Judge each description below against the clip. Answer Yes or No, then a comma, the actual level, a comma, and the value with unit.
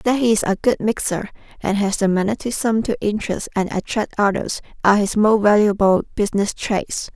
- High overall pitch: Yes, high, 210 Hz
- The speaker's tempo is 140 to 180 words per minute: Yes, average, 175 wpm